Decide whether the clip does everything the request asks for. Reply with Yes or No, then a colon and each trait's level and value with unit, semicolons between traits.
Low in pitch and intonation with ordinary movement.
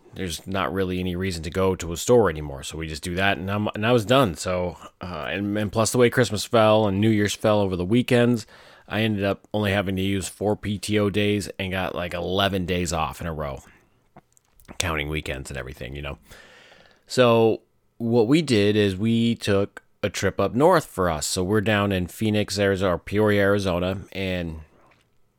Yes: low, 100 Hz; average, 3.1 semitones